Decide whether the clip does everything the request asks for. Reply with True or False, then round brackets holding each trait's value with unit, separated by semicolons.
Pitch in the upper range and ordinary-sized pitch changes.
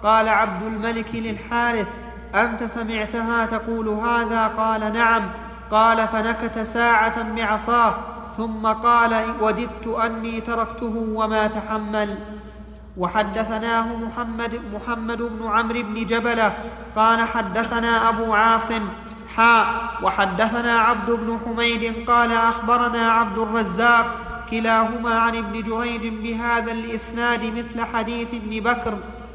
False (230 Hz; 0.8 semitones)